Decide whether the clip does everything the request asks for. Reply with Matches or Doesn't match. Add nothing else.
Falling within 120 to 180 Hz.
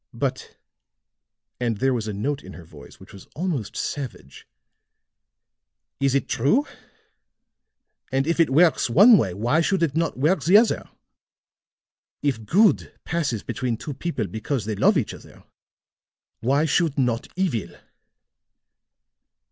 Matches